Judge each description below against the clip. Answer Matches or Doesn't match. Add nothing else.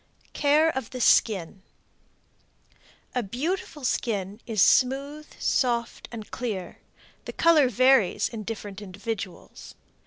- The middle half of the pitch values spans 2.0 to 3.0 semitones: Doesn't match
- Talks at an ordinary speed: Doesn't match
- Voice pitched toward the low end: Doesn't match